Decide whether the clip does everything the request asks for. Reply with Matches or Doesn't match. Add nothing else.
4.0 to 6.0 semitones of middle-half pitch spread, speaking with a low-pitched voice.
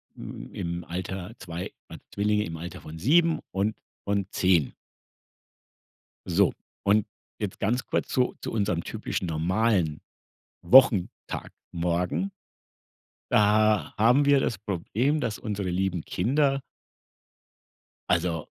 Matches